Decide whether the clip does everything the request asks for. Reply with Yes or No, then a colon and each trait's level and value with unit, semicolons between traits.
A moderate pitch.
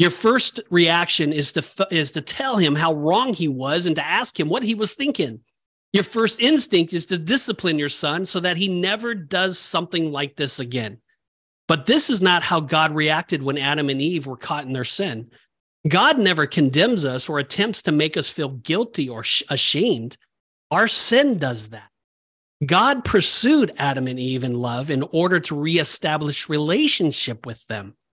Yes: medium, 160 Hz